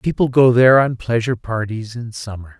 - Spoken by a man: Yes, male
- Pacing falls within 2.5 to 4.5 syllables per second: No, 5.5 syllables/s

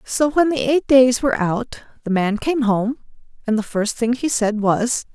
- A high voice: Yes, high, 240 Hz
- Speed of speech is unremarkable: No, fast, 210 wpm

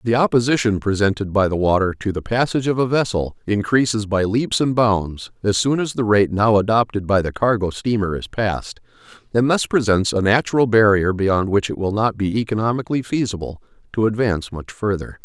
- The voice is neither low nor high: No, low, 105 Hz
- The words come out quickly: No, average, 190 wpm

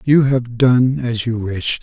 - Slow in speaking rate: No, average, 200 wpm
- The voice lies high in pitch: No, low, 120 Hz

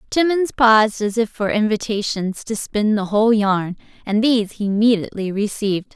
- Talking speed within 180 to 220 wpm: No, average, 160 wpm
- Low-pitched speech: No, high, 215 Hz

